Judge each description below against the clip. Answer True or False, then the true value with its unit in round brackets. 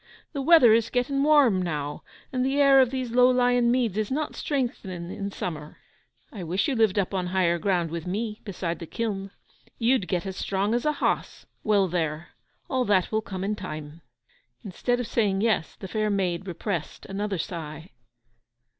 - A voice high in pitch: True (200 Hz)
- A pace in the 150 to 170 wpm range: False (180 wpm)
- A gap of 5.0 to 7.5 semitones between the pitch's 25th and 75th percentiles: True (5.4 semitones)